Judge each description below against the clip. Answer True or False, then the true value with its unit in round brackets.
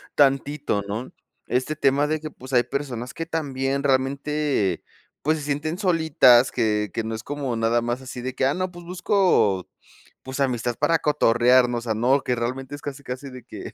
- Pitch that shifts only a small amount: False (3.4 semitones)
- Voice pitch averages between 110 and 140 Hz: True (135 Hz)